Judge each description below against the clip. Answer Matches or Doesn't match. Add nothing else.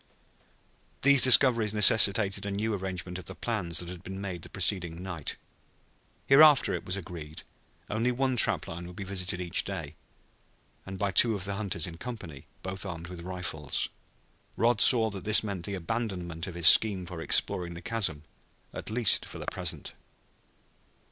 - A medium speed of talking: Matches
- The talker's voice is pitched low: Matches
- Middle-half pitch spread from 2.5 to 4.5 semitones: Matches